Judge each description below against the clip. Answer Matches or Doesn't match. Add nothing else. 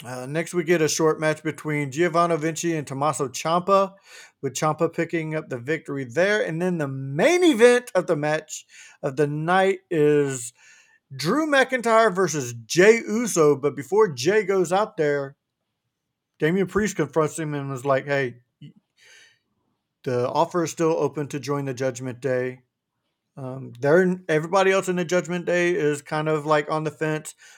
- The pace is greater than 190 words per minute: Doesn't match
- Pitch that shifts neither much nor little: Matches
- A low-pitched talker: Doesn't match